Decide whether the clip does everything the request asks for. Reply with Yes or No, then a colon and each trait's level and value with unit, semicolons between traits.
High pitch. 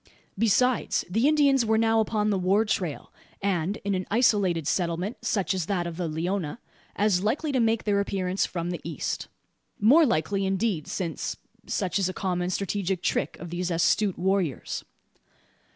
Yes: high, 195 Hz